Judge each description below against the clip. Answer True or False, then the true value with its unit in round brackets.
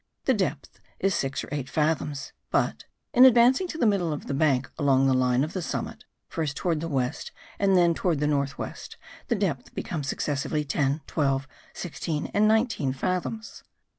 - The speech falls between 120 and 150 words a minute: False (180 wpm)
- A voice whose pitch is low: False (155 Hz)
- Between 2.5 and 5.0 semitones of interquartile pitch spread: False (5.6 semitones)